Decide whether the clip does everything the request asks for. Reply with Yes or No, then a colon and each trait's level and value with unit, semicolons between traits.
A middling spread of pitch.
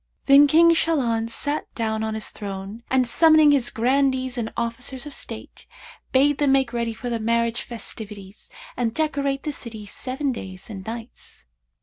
Yes: average, 3.8 semitones